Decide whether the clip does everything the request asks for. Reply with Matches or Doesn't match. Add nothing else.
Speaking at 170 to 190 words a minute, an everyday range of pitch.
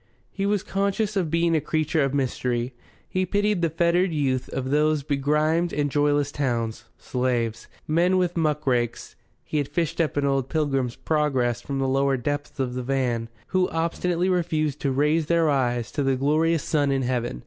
Matches